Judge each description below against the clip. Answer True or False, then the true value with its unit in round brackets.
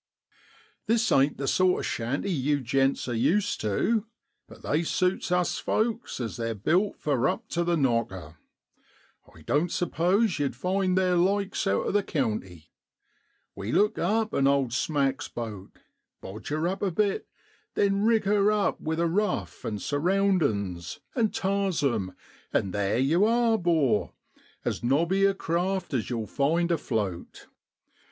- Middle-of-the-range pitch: True (165 Hz)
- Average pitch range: False (8.4 semitones)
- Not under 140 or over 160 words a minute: True (155 wpm)